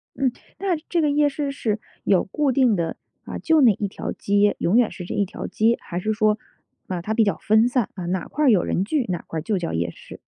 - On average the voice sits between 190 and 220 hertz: Yes, high, 215 Hz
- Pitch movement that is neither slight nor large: No, wide, 6.0 semitones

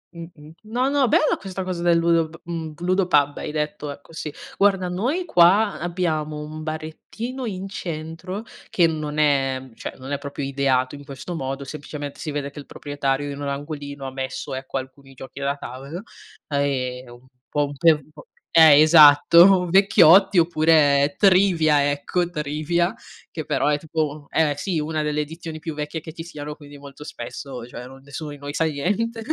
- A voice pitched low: No, medium, 155 Hz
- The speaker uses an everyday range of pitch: Yes, average, 3.3 semitones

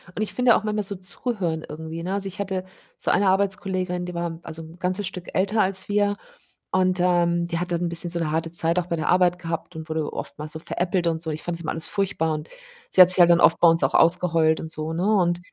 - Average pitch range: No, narrow, 2.3 semitones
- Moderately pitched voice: Yes, medium, 175 Hz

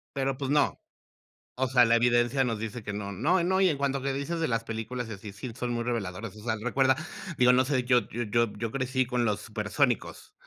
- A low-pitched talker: Yes, low, 125 Hz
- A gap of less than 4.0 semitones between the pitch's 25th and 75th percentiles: Yes, average, 3.0 semitones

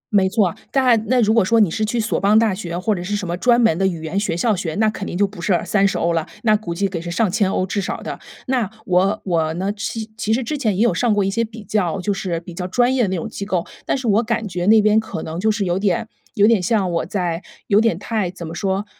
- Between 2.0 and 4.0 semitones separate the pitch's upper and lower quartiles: Yes, average, 3.5 semitones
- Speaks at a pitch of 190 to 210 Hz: Yes, high, 200 Hz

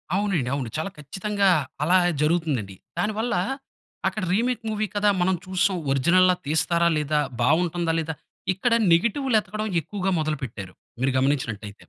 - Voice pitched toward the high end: No, medium, 175 Hz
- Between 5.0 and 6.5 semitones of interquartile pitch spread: Yes, wide, 5.6 semitones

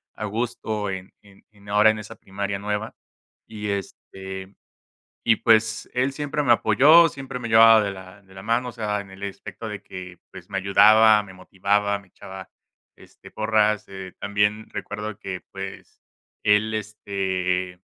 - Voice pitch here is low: Yes, low, 105 Hz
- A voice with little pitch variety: Yes, narrow, 2.2 semitones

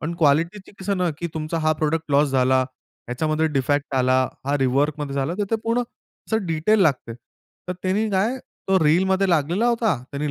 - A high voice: No, medium, 160 Hz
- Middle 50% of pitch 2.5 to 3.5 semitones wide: No, average, 4.9 semitones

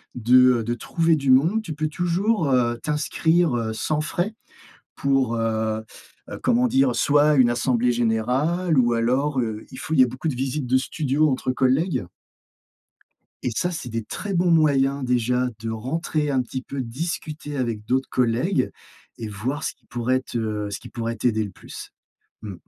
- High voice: No, low, 130 Hz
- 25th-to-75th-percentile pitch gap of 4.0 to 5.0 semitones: Yes, average, 4.6 semitones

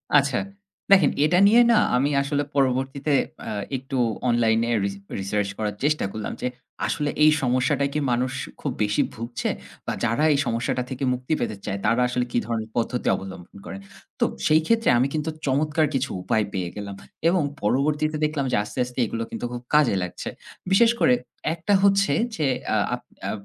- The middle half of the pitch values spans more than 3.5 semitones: Yes, average, 4.7 semitones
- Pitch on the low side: Yes, low, 130 Hz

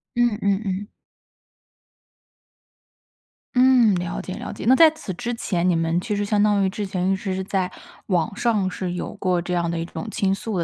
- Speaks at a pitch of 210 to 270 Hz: No, high, 195 Hz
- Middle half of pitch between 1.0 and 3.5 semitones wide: Yes, average, 2.8 semitones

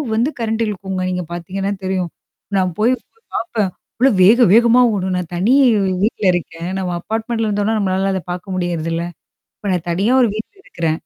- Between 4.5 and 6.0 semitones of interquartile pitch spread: No, average, 3.8 semitones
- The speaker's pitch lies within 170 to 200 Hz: Yes, high, 195 Hz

